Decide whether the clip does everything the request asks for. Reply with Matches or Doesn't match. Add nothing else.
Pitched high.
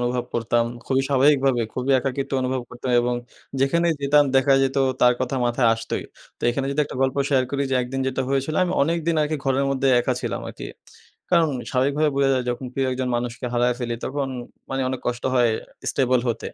Doesn't match